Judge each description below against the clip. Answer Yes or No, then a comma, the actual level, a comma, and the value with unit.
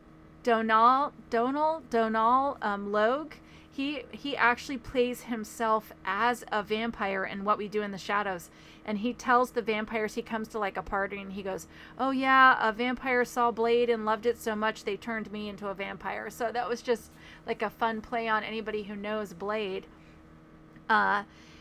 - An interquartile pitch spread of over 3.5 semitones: No, average, 2.7 semitones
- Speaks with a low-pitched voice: No, high, 220 Hz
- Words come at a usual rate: Yes, average, 180 wpm